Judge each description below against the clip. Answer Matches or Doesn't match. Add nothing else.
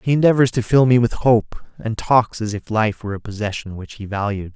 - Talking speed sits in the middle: Doesn't match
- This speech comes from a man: Matches